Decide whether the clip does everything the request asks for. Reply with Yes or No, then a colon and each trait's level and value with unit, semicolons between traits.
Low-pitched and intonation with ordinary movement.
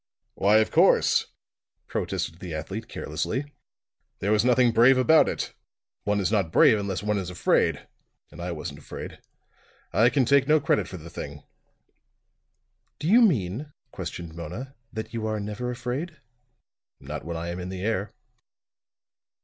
No: low, 105 Hz; wide, 5.9 semitones